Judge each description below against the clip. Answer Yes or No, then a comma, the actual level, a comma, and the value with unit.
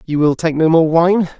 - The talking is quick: Yes, fast, 260 wpm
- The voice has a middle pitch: Yes, medium, 165 Hz